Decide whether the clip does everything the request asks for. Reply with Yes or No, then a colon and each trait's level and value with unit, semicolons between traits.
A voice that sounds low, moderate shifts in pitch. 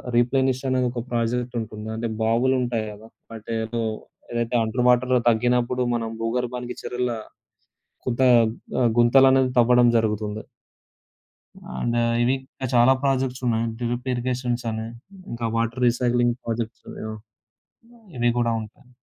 No: low, 120 Hz; narrow, 1.4 semitones